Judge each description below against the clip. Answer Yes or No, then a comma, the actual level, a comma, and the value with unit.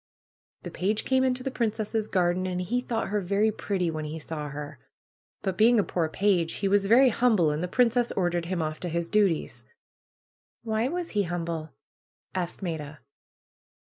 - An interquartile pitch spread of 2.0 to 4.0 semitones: No, average, 4.8 semitones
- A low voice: No, medium, 185 Hz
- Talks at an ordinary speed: Yes, average, 180 wpm